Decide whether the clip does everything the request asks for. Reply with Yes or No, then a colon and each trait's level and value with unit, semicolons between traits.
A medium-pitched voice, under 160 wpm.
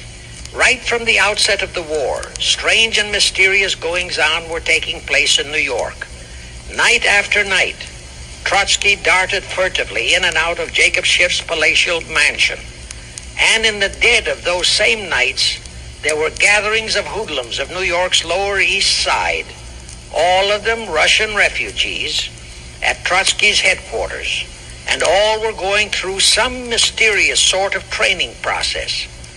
Yes: medium, 180 Hz; average, 140 wpm